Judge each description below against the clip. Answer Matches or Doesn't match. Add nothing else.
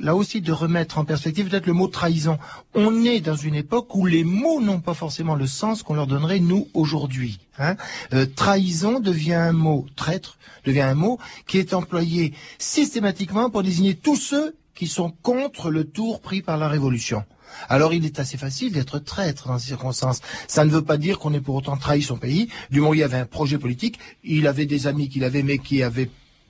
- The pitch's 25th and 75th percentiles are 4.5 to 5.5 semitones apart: Matches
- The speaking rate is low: Doesn't match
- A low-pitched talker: Doesn't match